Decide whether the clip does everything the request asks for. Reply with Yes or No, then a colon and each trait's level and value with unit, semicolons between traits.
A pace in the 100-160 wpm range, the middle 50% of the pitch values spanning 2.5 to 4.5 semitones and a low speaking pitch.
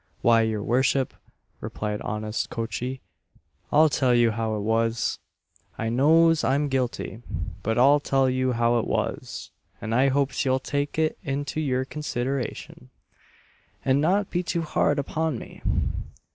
Yes: average, 145 wpm; average, 3.9 semitones; low, 130 Hz